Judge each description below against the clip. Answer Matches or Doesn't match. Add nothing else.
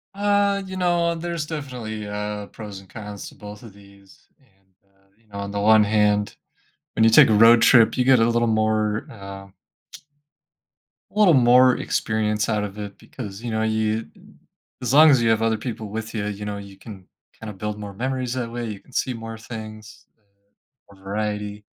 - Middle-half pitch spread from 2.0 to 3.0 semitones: Matches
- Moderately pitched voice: Doesn't match